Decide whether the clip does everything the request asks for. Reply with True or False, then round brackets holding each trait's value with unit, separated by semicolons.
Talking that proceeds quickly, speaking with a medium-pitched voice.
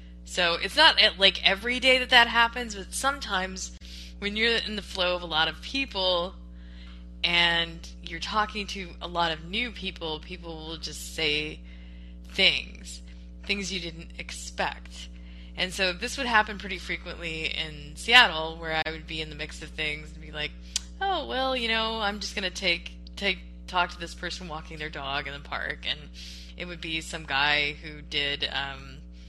False (180 wpm; 160 Hz)